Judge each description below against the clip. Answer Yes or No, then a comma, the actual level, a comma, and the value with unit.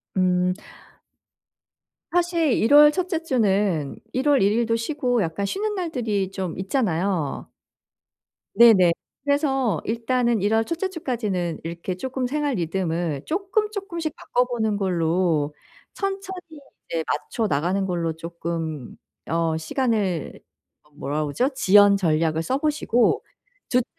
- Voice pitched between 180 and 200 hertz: No, high, 210 Hz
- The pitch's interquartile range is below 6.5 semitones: No, wide, 8.3 semitones